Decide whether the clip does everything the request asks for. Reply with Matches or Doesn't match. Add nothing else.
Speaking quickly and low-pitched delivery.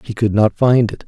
Matches